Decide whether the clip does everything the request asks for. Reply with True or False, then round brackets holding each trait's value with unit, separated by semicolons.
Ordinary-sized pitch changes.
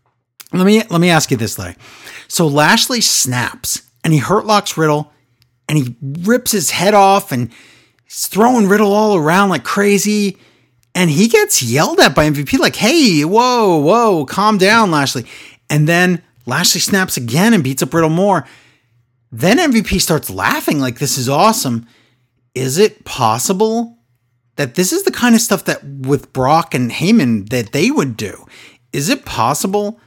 False (8.3 semitones)